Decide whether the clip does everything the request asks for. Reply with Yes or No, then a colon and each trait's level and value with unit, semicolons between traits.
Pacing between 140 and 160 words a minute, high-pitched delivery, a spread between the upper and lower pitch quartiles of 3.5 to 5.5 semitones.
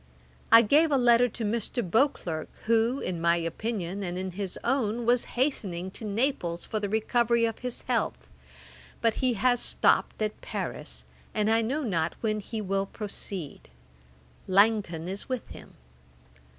Yes: average, 155 wpm; high, 215 Hz; average, 4.3 semitones